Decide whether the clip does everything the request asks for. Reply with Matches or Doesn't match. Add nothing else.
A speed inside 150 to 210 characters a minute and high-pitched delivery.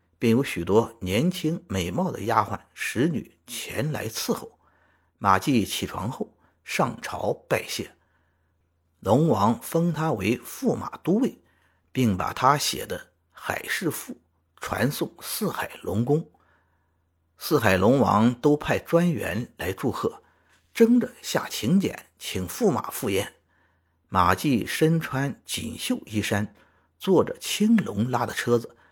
Doesn't match